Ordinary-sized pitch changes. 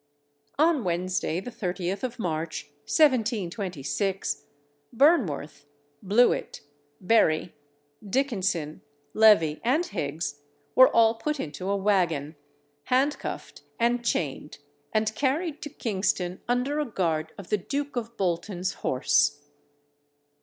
No: wide, 6.4 semitones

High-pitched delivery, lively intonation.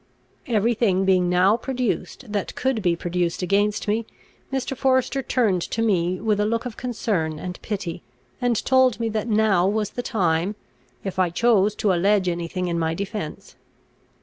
No: high, 205 Hz; average, 4.2 semitones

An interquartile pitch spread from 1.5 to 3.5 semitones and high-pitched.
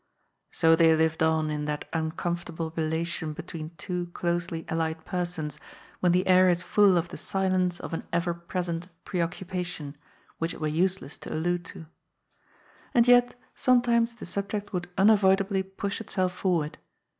No: average, 2.8 semitones; medium, 175 Hz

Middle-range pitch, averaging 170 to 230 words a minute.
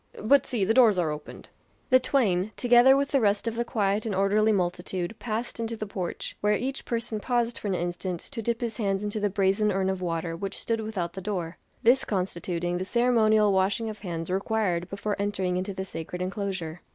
No: high, 200 Hz; fast, 205 wpm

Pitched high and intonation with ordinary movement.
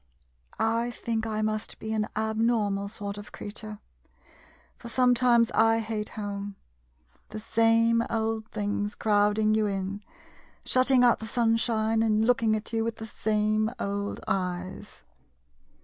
No: high, 220 Hz; narrow, 1.5 semitones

